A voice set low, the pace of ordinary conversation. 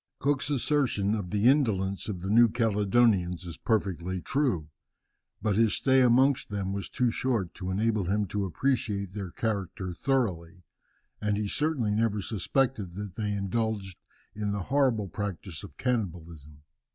Yes: low, 105 Hz; average, 150 wpm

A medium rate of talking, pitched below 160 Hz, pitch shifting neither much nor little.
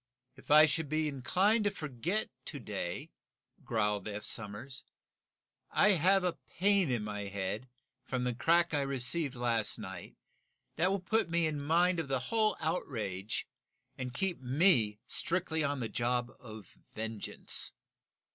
No: average, 145 wpm; low, 135 Hz; wide, 7.2 semitones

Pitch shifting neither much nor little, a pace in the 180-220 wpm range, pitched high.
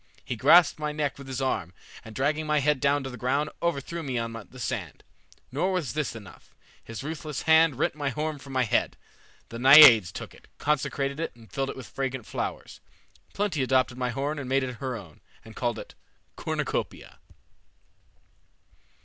No: average, 3.3 semitones; average, 185 wpm; low, 135 Hz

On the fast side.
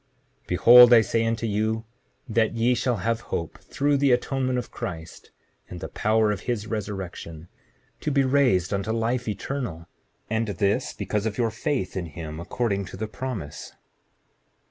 No: average, 160 wpm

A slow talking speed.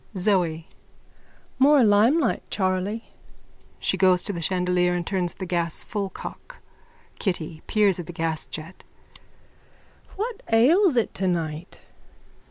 Yes: slow, 115 wpm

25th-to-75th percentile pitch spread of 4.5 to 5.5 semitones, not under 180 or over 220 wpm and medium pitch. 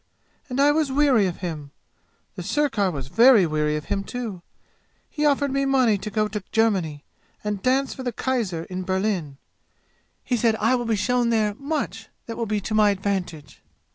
No: average, 5.2 semitones; average, 185 wpm; high, 215 Hz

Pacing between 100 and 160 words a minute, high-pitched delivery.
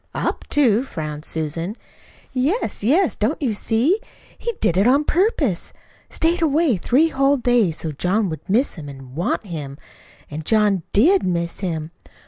Yes: average, 155 wpm; high, 215 Hz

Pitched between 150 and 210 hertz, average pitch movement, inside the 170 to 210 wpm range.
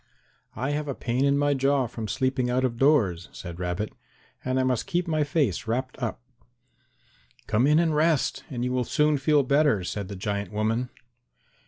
No: low, 130 Hz; average, 4.6 semitones; average, 185 wpm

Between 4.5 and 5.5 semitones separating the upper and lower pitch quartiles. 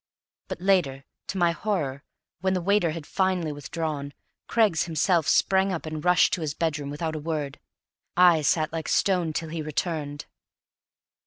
No: average, 3.2 semitones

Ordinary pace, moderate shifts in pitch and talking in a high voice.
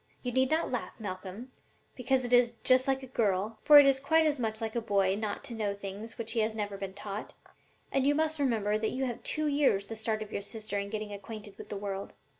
No: fast, 245 wpm; average, 4.2 semitones; high, 225 Hz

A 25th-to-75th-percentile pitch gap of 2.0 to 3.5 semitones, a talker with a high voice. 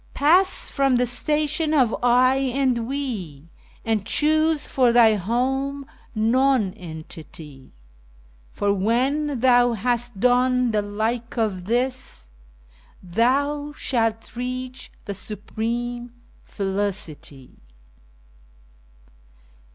No: average, 4.4 semitones; high, 240 Hz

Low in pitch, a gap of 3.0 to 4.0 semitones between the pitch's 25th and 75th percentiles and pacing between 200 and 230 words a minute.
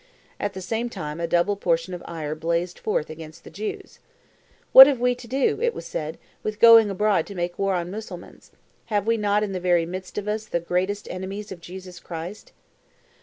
No: high, 190 Hz; average, 3.7 semitones; fast, 205 wpm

